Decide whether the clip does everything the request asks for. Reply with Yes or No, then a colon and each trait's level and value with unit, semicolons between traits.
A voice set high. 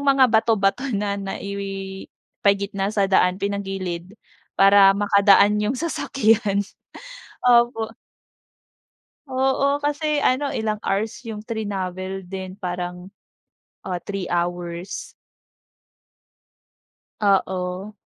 Yes: high, 200 Hz